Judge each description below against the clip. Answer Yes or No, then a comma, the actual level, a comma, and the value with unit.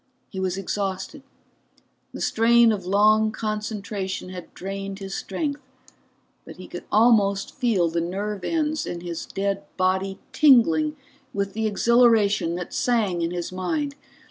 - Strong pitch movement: No, average, 3.2 semitones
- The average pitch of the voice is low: No, high, 200 Hz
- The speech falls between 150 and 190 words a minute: No, average, 140 wpm